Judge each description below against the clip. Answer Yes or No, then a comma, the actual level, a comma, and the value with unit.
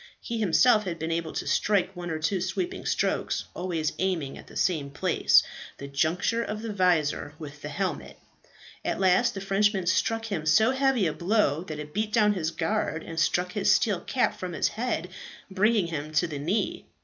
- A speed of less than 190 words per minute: No, average, 195 wpm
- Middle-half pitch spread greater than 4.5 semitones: Yes, average, 4.9 semitones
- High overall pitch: No, medium, 180 Hz